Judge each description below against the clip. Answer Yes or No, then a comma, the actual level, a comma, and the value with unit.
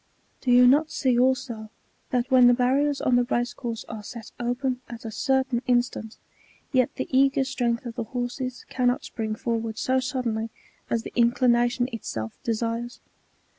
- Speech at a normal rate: Yes, average, 170 wpm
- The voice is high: Yes, high, 245 Hz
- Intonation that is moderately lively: No, narrow, 1.8 semitones